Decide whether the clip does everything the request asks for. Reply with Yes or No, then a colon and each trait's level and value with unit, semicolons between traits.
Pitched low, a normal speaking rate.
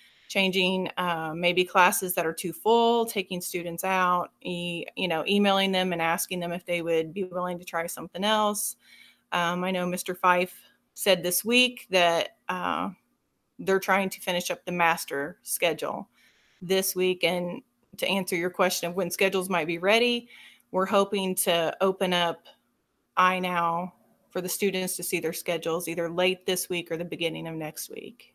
No: medium, 180 Hz; average, 175 wpm